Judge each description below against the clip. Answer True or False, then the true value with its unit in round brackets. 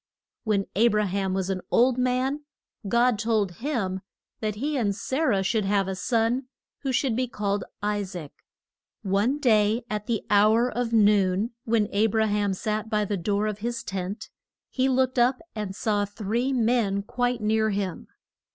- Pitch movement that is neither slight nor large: True (3.2 semitones)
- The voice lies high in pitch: True (215 Hz)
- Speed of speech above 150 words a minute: True (175 wpm)